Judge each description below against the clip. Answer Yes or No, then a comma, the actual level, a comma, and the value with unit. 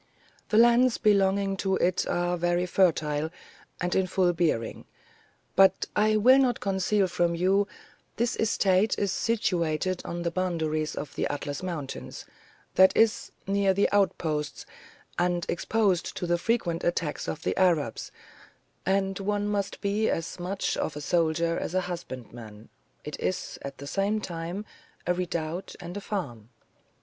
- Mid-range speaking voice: Yes, medium, 180 Hz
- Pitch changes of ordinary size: Yes, average, 3.2 semitones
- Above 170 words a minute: No, average, 150 wpm